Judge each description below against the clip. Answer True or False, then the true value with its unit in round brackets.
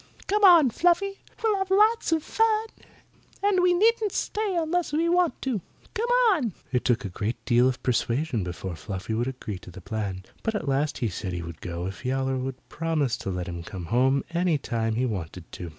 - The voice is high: False (135 Hz)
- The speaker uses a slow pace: False (205 wpm)